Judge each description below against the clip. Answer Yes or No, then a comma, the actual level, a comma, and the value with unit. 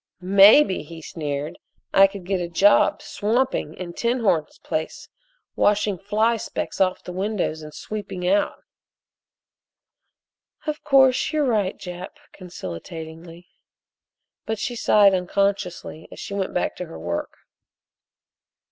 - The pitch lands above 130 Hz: Yes, high, 190 Hz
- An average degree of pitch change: Yes, average, 3.6 semitones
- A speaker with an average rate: No, slow, 120 wpm